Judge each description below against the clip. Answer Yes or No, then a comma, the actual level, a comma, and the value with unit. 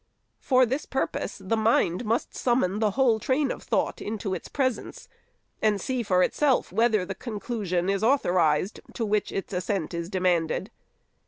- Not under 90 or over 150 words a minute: No, average, 160 wpm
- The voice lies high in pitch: Yes, high, 210 Hz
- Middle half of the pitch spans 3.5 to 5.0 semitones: Yes, average, 4.7 semitones